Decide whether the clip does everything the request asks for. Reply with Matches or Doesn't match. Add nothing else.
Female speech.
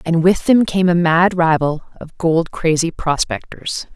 Matches